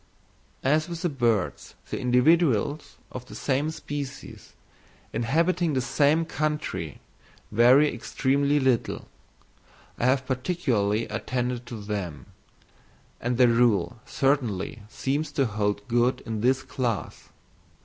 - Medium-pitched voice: No, low, 130 Hz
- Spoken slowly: Yes, slow, 110 wpm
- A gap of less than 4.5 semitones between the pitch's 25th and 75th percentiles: Yes, average, 4.0 semitones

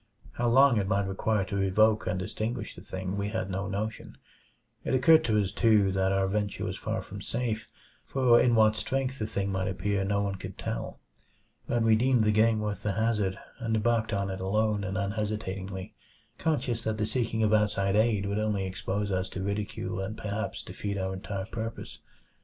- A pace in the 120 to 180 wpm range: No, average, 195 wpm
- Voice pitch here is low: Yes, low, 105 Hz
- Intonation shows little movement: Yes, narrow, 2.3 semitones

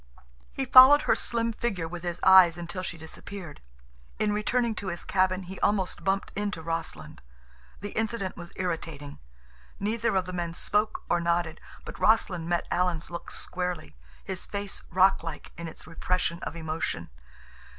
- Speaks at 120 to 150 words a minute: No, average, 160 wpm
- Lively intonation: No, average, 3.2 semitones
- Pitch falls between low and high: Yes, medium, 180 Hz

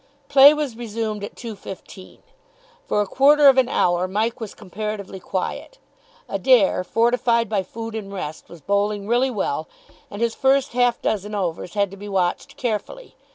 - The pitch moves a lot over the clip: No, average, 3.7 semitones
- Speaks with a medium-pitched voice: No, high, 215 Hz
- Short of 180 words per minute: Yes, average, 160 wpm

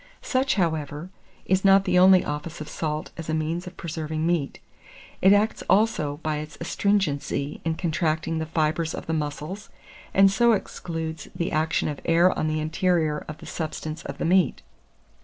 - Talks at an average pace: Yes, average, 175 wpm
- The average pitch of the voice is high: No, medium, 160 Hz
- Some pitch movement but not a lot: Yes, average, 3.1 semitones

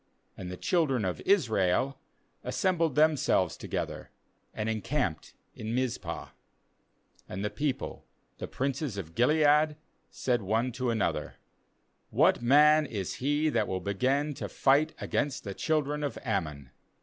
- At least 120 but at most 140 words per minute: Yes, slow, 135 wpm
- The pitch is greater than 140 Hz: No, low, 130 Hz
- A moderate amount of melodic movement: No, wide, 6.3 semitones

